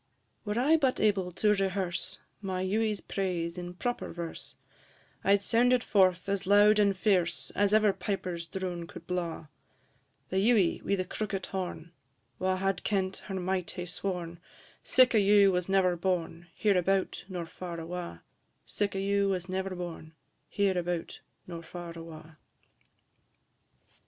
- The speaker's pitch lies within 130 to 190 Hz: Yes, medium, 185 Hz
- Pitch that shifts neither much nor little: No, narrow, 2.3 semitones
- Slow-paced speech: No, average, 150 wpm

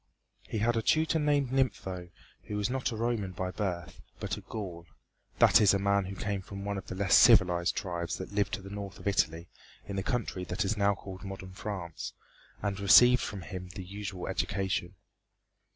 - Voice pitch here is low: Yes, low, 100 Hz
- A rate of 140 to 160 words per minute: No, average, 200 wpm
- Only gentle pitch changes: Yes, narrow, 2.1 semitones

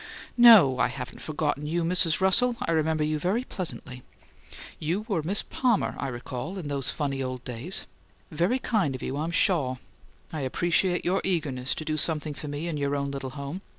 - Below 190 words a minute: No, average, 200 wpm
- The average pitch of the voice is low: No, medium, 155 Hz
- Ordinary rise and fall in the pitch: Yes, average, 4.3 semitones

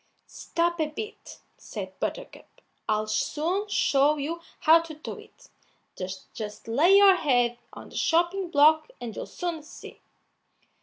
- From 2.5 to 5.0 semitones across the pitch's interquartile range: No, wide, 5.5 semitones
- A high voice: Yes, very high, 315 Hz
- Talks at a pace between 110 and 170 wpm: Yes, average, 140 wpm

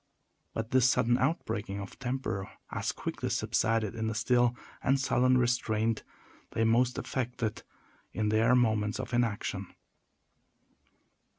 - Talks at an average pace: No, slow, 120 wpm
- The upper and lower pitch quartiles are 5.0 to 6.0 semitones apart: No, narrow, 2.4 semitones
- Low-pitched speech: Yes, low, 115 Hz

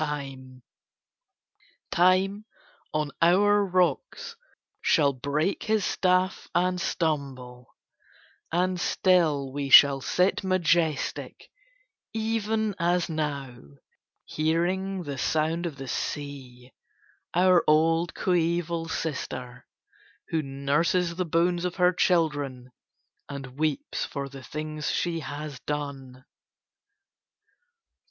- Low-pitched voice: No, medium, 160 Hz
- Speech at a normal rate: No, slow, 95 wpm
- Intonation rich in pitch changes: No, average, 4.2 semitones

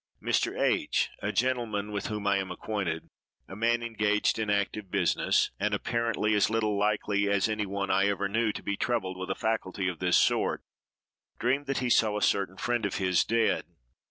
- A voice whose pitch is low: Yes, low, 105 Hz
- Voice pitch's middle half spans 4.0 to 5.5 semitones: No, narrow, 2.4 semitones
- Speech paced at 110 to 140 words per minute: No, average, 185 wpm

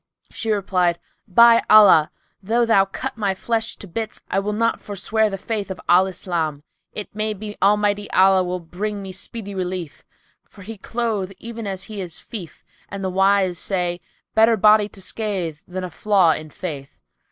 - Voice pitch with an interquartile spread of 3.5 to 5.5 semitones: No, average, 2.7 semitones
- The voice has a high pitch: Yes, high, 195 Hz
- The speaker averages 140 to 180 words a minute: Yes, average, 175 wpm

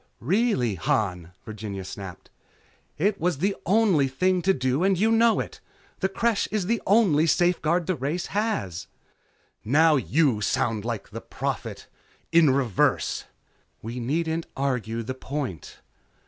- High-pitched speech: No, medium, 150 Hz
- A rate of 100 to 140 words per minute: Yes, slow, 135 wpm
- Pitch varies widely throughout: Yes, wide, 8.3 semitones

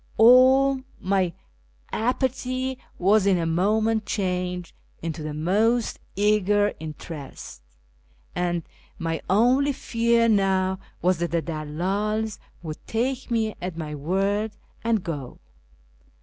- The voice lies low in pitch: No, high, 195 Hz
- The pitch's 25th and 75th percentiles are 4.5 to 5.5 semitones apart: Yes, average, 4.9 semitones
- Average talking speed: No, slow, 110 wpm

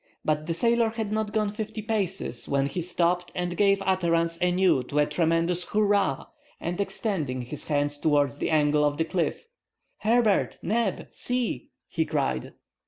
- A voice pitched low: No, medium, 175 Hz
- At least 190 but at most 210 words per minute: No, average, 160 wpm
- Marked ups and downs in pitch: Yes, wide, 5.7 semitones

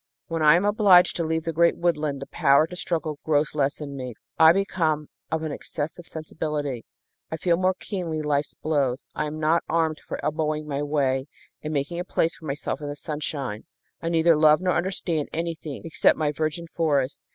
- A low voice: No, medium, 155 Hz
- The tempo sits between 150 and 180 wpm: No, average, 195 wpm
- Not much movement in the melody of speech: Yes, narrow, 2.2 semitones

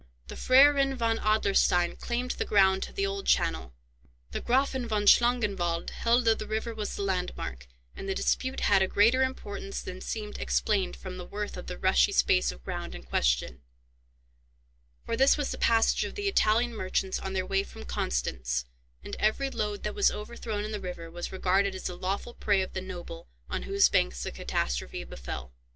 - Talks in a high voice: Yes, high, 200 Hz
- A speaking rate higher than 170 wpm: Yes, average, 190 wpm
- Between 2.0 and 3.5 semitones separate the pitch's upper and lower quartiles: No, average, 4.3 semitones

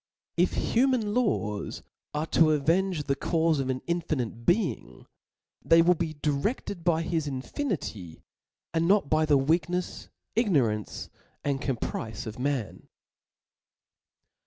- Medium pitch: Yes, medium, 155 Hz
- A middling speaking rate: No, slow, 120 wpm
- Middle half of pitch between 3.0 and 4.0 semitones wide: No, average, 4.7 semitones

